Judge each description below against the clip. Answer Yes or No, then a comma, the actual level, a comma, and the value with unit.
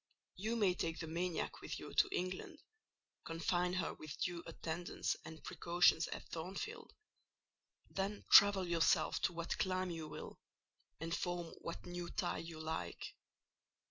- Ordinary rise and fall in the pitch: No, narrow, 1.9 semitones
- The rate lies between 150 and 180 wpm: No, average, 140 wpm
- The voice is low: No, medium, 175 Hz